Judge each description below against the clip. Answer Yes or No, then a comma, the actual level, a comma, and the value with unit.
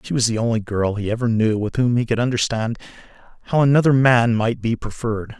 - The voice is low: Yes, low, 115 Hz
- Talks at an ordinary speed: No, fast, 210 wpm